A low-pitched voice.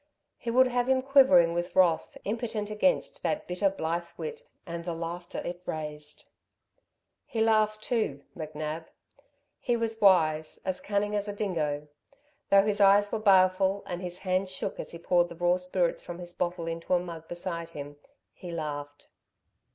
No: medium, 180 Hz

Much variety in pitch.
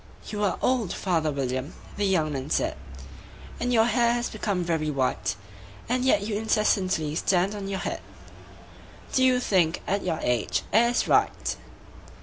Yes: wide, 6.0 semitones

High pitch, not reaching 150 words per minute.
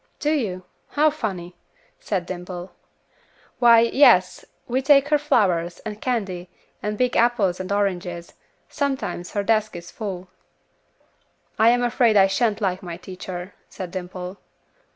Yes: high, 200 Hz; slow, 135 wpm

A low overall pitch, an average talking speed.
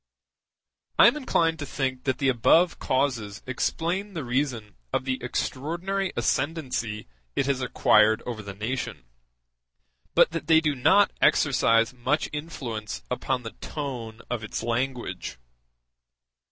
No: low, 130 Hz; slow, 130 wpm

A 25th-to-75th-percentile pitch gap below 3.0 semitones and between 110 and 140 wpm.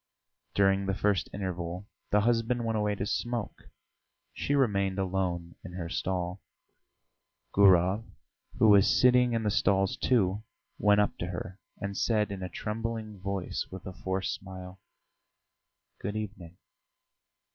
Yes: narrow, 2.4 semitones; slow, 135 wpm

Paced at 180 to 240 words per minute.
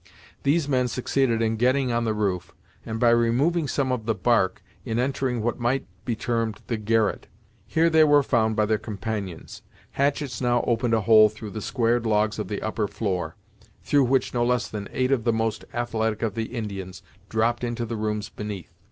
Yes: average, 195 wpm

